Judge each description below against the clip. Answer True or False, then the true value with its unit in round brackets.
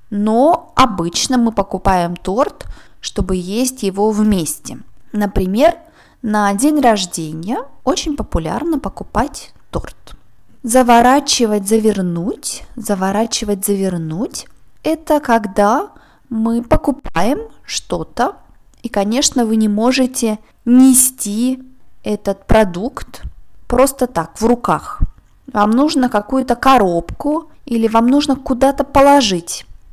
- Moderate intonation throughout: True (4.5 semitones)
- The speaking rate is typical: False (95 wpm)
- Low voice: False (235 Hz)